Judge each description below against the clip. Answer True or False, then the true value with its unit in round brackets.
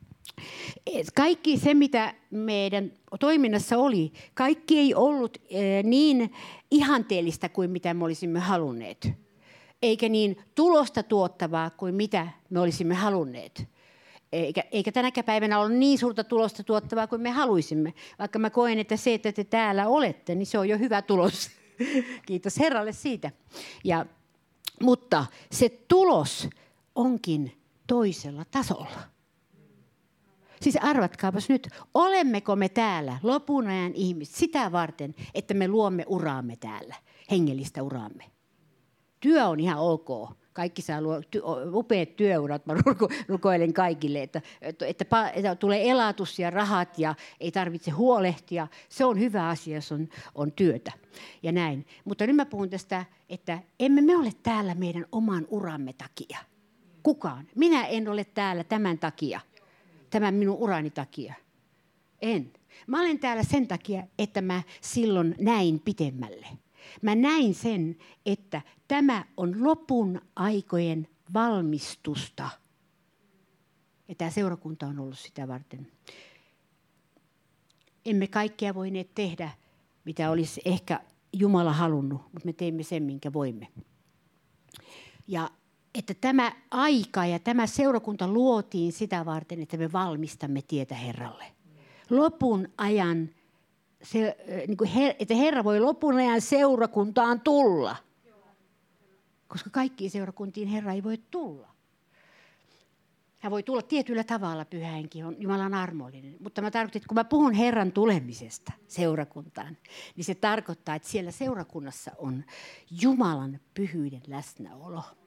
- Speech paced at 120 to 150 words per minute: True (125 wpm)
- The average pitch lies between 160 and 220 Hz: True (190 Hz)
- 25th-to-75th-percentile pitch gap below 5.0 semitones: False (5.5 semitones)